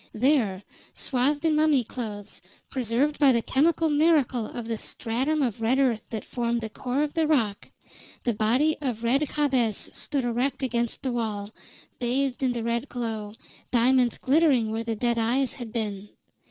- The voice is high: Yes, high, 245 Hz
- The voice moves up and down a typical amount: Yes, average, 3.4 semitones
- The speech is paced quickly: No, average, 165 wpm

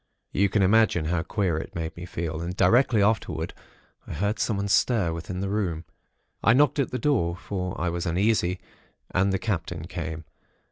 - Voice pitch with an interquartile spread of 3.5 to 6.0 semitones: Yes, average, 3.9 semitones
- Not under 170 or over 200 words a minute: Yes, average, 180 wpm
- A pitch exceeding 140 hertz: No, very low, 90 Hz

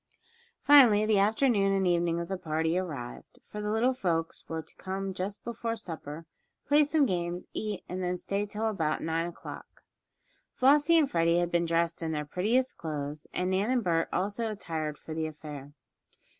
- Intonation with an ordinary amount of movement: Yes, average, 4.6 semitones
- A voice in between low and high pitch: Yes, medium, 180 Hz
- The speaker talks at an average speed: Yes, average, 180 wpm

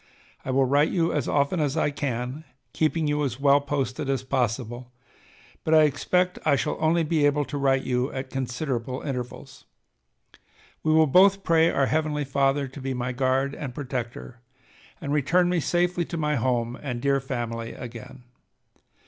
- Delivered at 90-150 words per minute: No, average, 170 wpm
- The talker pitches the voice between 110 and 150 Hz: Yes, medium, 140 Hz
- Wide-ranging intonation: No, average, 3.2 semitones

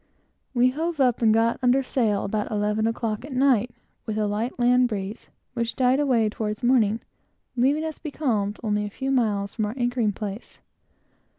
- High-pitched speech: Yes, high, 230 Hz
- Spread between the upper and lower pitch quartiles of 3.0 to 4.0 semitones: Yes, average, 3.3 semitones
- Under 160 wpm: No, average, 175 wpm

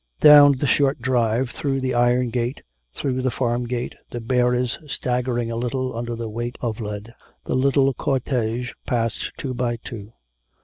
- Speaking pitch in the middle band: No, low, 125 Hz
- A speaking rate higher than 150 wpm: Yes, average, 165 wpm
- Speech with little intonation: Yes, narrow, 1.8 semitones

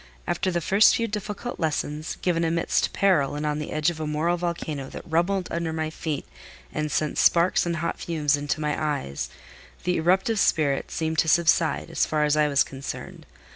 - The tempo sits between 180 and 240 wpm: Yes, average, 190 wpm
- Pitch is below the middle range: No, medium, 160 Hz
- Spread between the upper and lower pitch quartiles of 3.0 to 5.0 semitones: No, narrow, 2.4 semitones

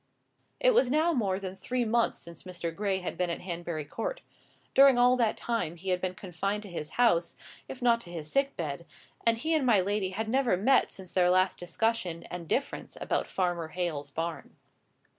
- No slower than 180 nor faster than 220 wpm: Yes, average, 200 wpm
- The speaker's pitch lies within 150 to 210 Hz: Yes, high, 190 Hz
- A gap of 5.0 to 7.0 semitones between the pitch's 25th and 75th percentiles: Yes, wide, 5.5 semitones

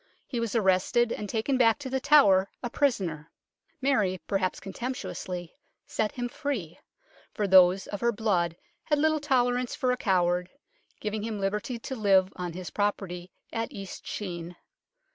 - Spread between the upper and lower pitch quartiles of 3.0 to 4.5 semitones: No, average, 4.9 semitones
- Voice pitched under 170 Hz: No, high, 210 Hz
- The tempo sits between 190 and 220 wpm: No, average, 155 wpm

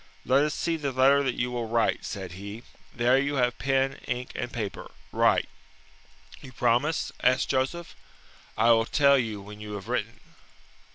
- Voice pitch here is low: Yes, low, 125 Hz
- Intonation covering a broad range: No, average, 3.1 semitones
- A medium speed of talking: Yes, average, 170 wpm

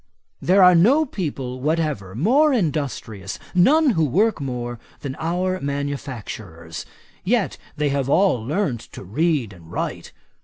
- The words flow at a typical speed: No, slow, 130 wpm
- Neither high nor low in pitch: Yes, medium, 145 Hz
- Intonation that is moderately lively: No, wide, 7.2 semitones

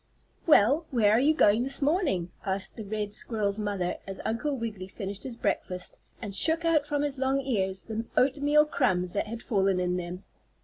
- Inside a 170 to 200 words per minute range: Yes, average, 185 wpm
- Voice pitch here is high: Yes, high, 220 Hz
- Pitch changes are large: Yes, wide, 6.0 semitones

